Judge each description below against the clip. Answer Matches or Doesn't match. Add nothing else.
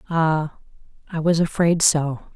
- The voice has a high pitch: Doesn't match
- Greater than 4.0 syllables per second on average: Doesn't match